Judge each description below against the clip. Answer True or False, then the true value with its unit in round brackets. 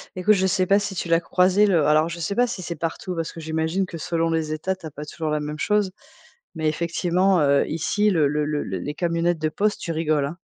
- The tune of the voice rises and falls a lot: False (3.1 semitones)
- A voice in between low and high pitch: True (165 Hz)